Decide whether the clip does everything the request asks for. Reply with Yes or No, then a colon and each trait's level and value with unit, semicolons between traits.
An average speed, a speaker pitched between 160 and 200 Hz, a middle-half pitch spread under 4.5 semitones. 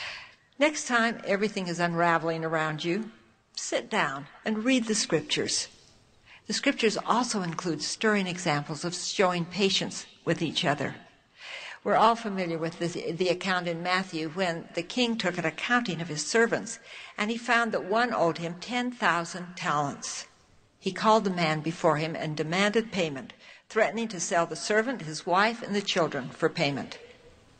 No: average, 160 wpm; medium, 185 Hz; average, 4.8 semitones